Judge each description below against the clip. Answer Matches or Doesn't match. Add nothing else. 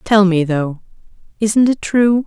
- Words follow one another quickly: Doesn't match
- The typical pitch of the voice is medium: Doesn't match